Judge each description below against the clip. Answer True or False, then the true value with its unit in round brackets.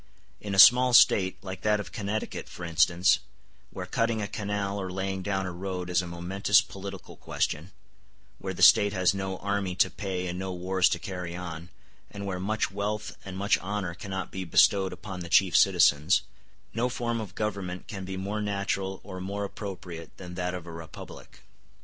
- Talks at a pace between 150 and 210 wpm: True (185 wpm)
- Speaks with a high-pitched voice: False (95 Hz)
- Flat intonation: True (2.0 semitones)